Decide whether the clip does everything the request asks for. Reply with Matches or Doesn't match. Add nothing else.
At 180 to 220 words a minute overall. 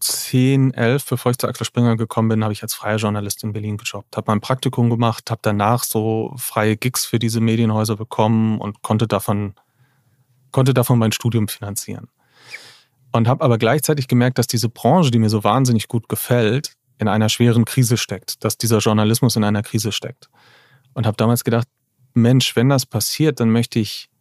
Matches